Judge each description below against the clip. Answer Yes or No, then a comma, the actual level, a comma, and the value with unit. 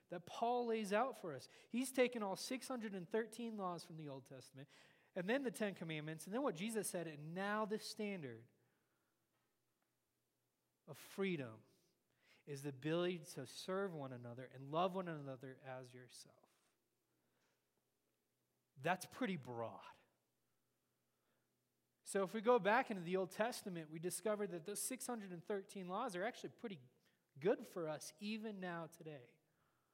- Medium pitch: Yes, medium, 180 Hz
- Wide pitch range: Yes, wide, 6.8 semitones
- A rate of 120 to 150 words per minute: Yes, average, 140 wpm